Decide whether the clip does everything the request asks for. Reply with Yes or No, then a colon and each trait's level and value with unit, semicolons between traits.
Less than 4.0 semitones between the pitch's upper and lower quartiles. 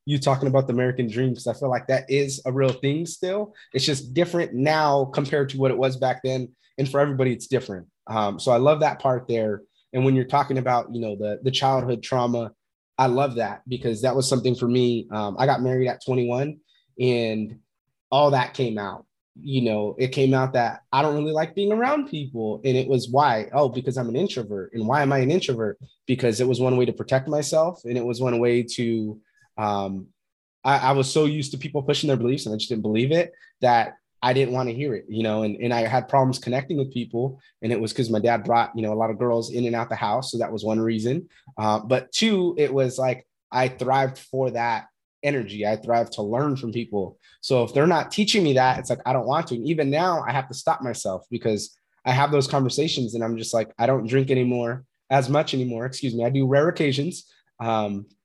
Yes: average, 2.8 semitones